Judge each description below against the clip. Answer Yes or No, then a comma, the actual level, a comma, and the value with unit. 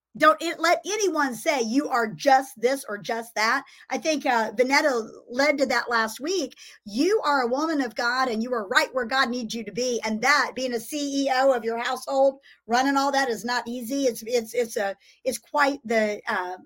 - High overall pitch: Yes, very high, 255 Hz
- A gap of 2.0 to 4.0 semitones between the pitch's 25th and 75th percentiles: Yes, average, 3.3 semitones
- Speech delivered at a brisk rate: Yes, fast, 215 wpm